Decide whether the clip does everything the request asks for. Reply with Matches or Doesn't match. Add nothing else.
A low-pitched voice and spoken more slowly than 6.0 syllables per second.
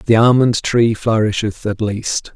Matches